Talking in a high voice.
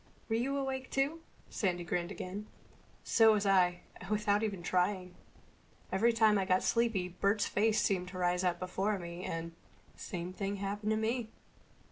Yes: high, 200 Hz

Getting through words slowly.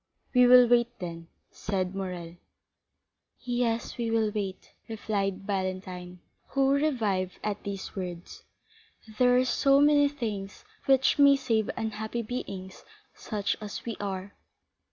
Yes: slow, 125 wpm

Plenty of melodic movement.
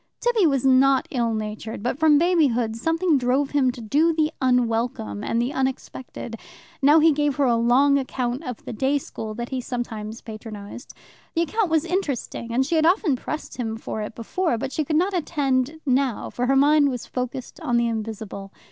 No: average, 4.2 semitones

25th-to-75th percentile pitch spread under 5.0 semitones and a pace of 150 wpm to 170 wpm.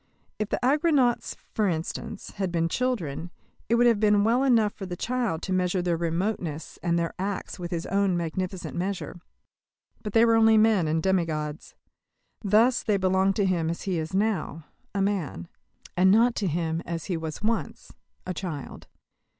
No: average, 4.3 semitones; average, 180 wpm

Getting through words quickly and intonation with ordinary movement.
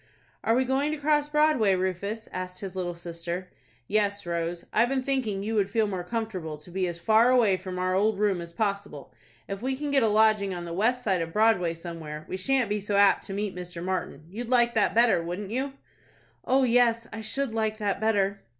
Yes: fast, 215 wpm; average, 4.2 semitones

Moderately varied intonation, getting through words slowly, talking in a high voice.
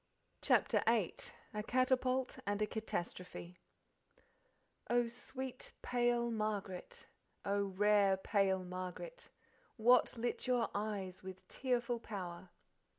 Yes: average, 4.2 semitones; slow, 100 wpm; high, 215 Hz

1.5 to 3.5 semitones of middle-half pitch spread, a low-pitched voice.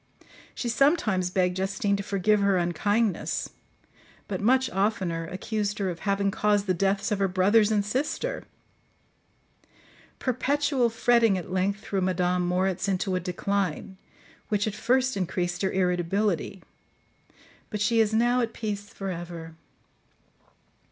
No: average, 3.0 semitones; high, 200 Hz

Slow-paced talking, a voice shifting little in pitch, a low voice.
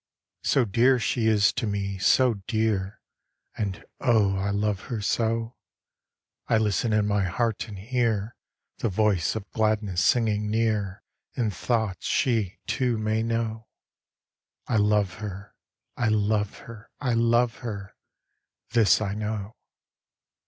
Yes: slow, 130 wpm; narrow, 2.2 semitones; low, 110 Hz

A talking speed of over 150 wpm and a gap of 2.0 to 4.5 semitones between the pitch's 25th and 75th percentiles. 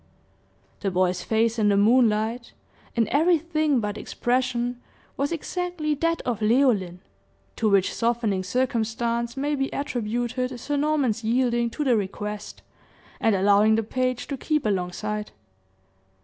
No: slow, 135 wpm; average, 3.9 semitones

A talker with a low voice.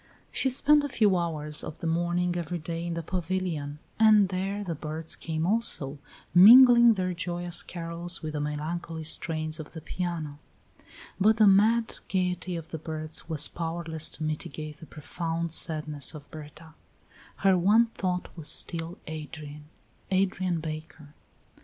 No: medium, 170 Hz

